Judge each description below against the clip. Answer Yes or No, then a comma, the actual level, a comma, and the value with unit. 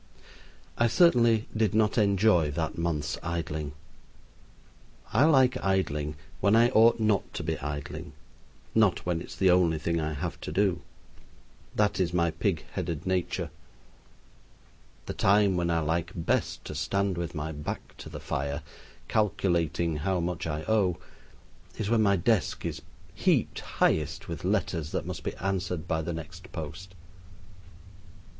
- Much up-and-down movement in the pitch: No, average, 4.0 semitones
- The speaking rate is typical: Yes, average, 150 wpm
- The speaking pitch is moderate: No, very low, 90 Hz